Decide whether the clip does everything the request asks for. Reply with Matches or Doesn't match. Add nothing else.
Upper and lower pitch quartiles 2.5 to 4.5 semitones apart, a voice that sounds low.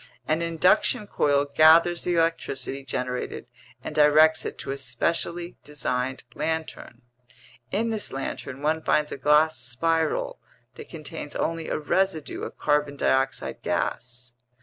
Doesn't match